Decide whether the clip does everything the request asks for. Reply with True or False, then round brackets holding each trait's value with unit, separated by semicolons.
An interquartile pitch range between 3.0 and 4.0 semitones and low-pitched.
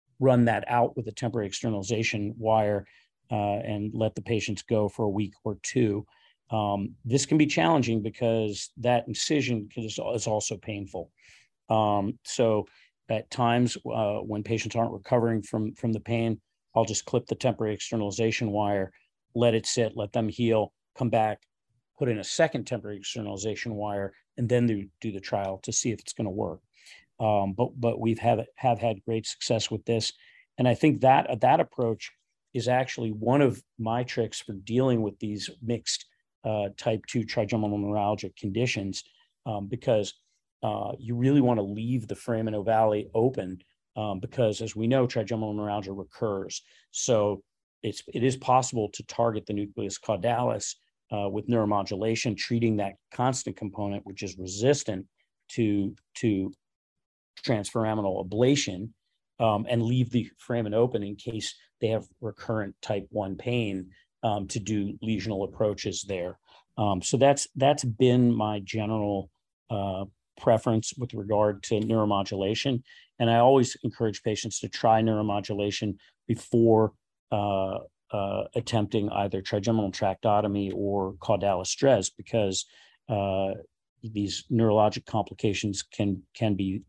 False (2.5 semitones; 110 Hz)